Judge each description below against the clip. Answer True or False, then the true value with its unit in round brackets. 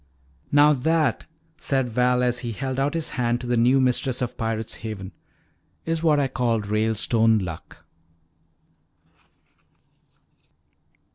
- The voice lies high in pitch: False (125 Hz)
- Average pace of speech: False (125 wpm)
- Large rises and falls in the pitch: False (3.2 semitones)